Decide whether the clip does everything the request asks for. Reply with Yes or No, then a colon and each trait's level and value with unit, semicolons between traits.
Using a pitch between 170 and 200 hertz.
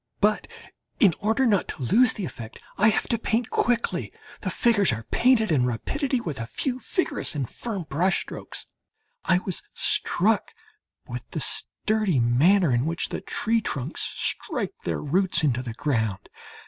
Yes: high, 190 Hz